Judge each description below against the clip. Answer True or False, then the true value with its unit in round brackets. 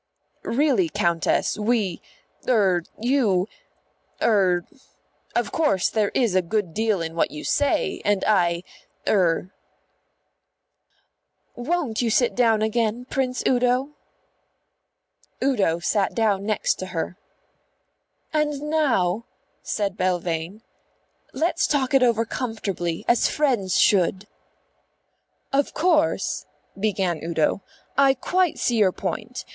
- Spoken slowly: True (110 wpm)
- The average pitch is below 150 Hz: False (215 Hz)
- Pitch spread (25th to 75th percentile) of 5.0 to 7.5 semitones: True (5.5 semitones)